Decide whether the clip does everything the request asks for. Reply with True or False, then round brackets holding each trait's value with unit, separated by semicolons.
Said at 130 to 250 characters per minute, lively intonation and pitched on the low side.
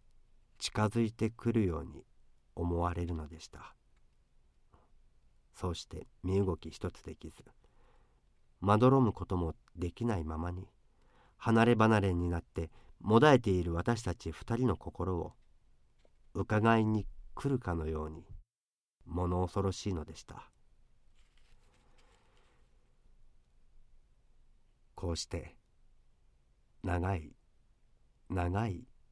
False (195 characters per minute; 4.4 semitones; 90 Hz)